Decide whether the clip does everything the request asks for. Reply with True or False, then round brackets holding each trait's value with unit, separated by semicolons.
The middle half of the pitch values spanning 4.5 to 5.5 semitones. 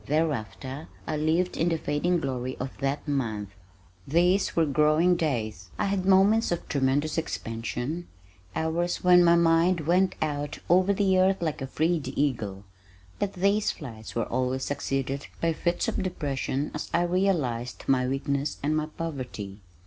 True (4.8 semitones)